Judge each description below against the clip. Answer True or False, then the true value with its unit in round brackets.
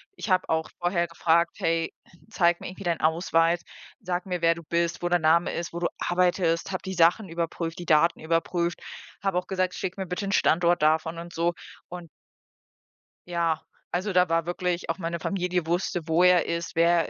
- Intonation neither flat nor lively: False (1.4 semitones)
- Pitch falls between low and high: True (170 Hz)